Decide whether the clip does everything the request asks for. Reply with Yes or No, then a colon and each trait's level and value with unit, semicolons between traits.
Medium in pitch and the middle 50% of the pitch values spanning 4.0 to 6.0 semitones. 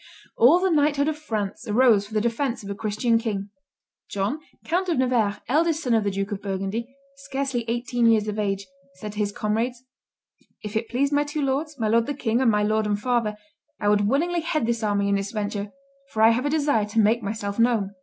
No: high, 225 Hz; average, 4.5 semitones